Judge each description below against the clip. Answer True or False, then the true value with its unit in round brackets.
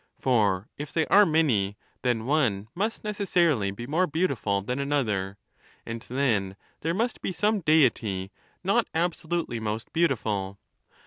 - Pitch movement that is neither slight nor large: False (8.3 semitones)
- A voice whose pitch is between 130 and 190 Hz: True (135 Hz)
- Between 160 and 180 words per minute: False (140 wpm)